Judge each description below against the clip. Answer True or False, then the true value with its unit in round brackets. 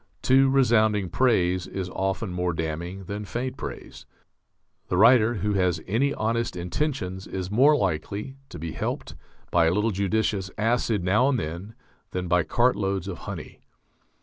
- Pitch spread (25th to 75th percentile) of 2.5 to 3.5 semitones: False (4.4 semitones)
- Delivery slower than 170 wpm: True (150 wpm)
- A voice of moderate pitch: False (100 Hz)